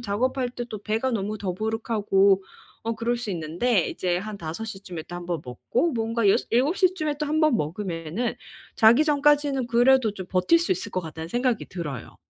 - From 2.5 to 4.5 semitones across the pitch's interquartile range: No, wide, 5.4 semitones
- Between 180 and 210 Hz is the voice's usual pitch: No, high, 220 Hz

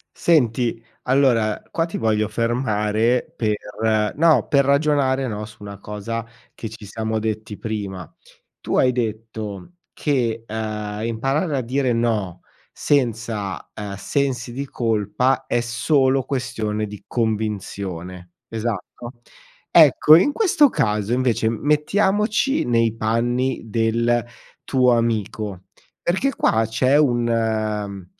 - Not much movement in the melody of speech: No, average, 3.4 semitones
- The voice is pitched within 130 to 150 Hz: No, low, 115 Hz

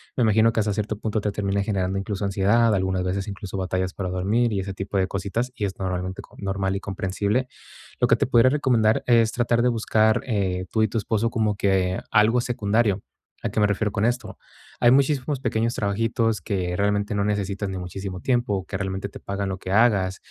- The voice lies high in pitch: No, low, 100 Hz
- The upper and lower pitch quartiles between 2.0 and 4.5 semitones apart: Yes, average, 2.8 semitones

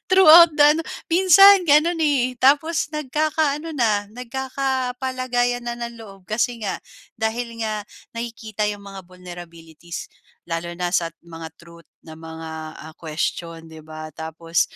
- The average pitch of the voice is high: Yes, high, 230 Hz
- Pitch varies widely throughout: Yes, wide, 8.4 semitones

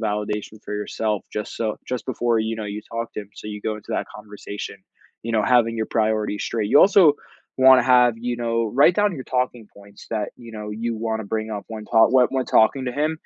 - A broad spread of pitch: No, narrow, 2.6 semitones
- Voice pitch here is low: Yes, low, 110 Hz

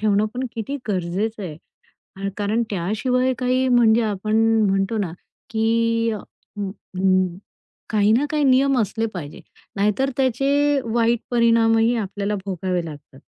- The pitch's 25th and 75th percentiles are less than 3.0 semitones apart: No, average, 3.4 semitones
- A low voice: No, high, 225 Hz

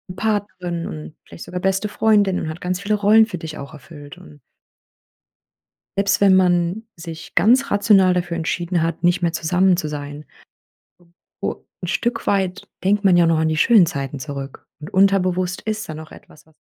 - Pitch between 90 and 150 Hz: No, medium, 180 Hz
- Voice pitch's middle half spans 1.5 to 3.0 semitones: No, average, 3.8 semitones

